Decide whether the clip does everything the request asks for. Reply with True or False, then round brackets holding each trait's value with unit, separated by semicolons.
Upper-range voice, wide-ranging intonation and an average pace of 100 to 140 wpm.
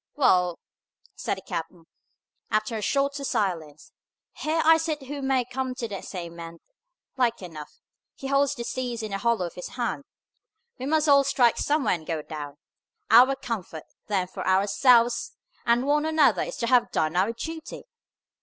False (235 Hz; 7.2 semitones; 170 wpm)